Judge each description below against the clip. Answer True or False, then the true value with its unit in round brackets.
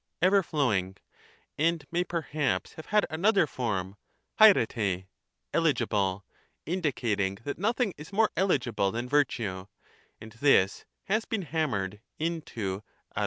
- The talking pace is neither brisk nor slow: False (120 wpm)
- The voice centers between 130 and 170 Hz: True (140 Hz)